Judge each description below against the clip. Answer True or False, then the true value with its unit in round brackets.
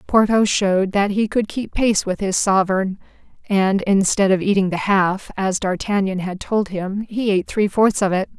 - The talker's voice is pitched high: True (195 Hz)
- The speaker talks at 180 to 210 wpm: True (195 wpm)